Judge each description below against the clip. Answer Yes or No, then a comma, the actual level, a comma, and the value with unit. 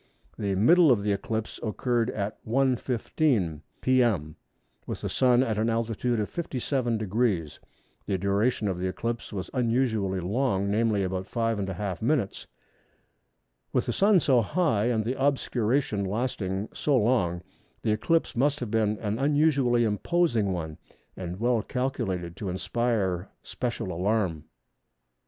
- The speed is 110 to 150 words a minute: Yes, slow, 135 wpm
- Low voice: Yes, low, 110 Hz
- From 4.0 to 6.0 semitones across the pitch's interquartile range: Yes, average, 4.3 semitones